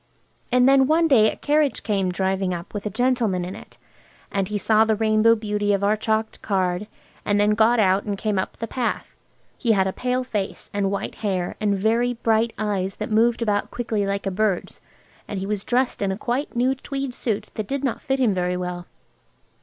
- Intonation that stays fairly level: No, average, 3.4 semitones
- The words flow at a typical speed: No, fast, 210 wpm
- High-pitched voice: Yes, high, 215 Hz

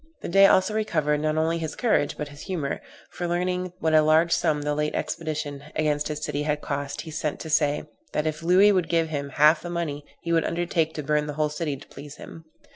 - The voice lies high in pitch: No, medium, 155 Hz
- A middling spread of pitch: No, narrow, 2.2 semitones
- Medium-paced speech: No, fast, 230 wpm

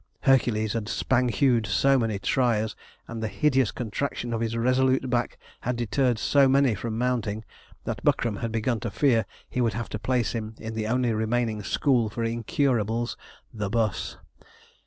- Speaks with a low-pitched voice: Yes, low, 115 Hz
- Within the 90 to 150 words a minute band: No, average, 170 wpm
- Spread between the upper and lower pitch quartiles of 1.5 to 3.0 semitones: Yes, narrow, 2.4 semitones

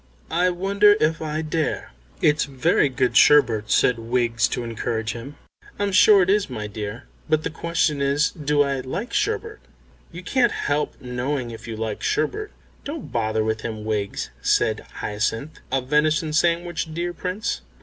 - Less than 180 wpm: Yes, average, 160 wpm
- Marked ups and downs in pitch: Yes, wide, 6.5 semitones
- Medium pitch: Yes, medium, 145 Hz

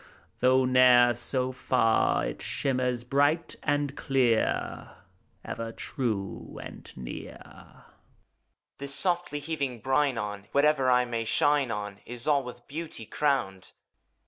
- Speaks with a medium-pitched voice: No, low, 130 Hz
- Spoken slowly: Yes, slow, 120 wpm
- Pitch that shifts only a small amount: No, average, 3.5 semitones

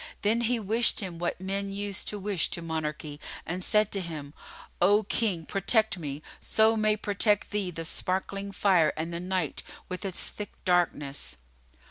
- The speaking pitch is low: No, high, 190 Hz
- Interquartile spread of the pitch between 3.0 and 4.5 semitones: Yes, average, 3.7 semitones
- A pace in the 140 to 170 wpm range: Yes, average, 165 wpm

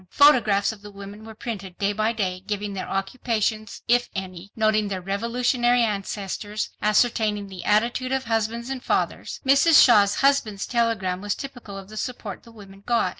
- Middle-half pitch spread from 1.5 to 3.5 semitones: Yes, average, 3.1 semitones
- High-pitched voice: Yes, high, 215 Hz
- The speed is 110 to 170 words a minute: Yes, average, 165 wpm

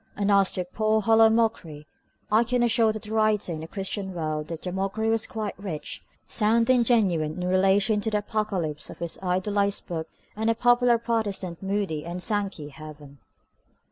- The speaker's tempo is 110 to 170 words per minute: No, average, 180 wpm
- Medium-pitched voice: No, high, 200 Hz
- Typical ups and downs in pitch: Yes, average, 4.2 semitones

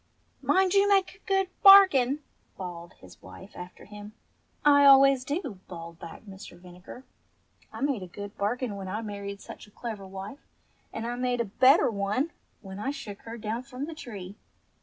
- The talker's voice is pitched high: Yes, high, 225 Hz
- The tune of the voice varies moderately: No, wide, 5.9 semitones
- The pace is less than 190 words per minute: Yes, average, 180 wpm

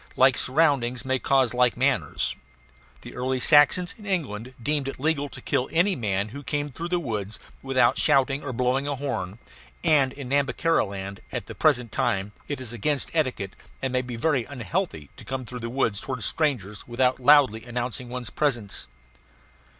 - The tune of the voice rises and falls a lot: No, average, 3.3 semitones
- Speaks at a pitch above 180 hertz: No, low, 130 Hz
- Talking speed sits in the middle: Yes, average, 175 wpm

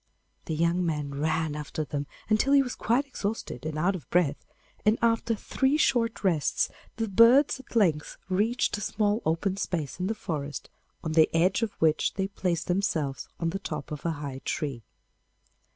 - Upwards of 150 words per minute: Yes, average, 180 wpm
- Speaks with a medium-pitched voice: Yes, medium, 180 Hz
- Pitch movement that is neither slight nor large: No, wide, 6.1 semitones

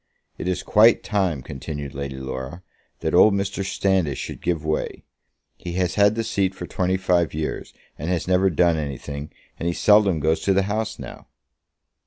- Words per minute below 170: No, average, 180 wpm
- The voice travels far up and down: No, average, 4.1 semitones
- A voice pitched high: No, very low, 90 Hz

